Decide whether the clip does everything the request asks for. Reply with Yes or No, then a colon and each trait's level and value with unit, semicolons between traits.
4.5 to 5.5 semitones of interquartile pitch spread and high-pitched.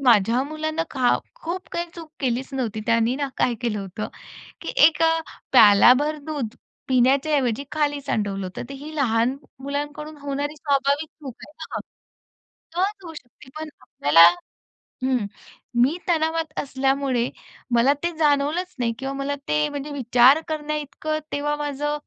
No: average, 3.8 semitones; very high, 280 Hz